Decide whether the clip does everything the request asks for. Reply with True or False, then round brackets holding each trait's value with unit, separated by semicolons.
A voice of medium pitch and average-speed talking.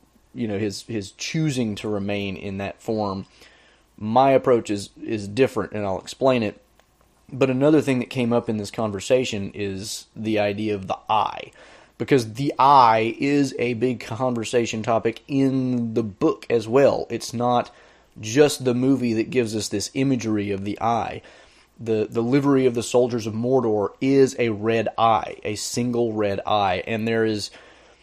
False (115 Hz; 170 wpm)